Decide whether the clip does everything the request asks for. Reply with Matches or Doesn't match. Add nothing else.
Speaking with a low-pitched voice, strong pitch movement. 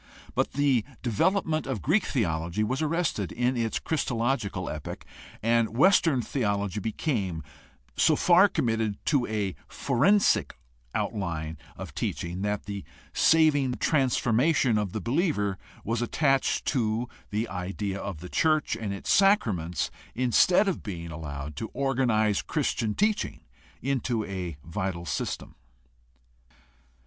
Matches